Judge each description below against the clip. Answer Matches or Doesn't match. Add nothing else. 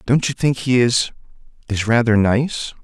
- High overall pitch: Doesn't match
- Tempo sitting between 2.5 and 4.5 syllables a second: Matches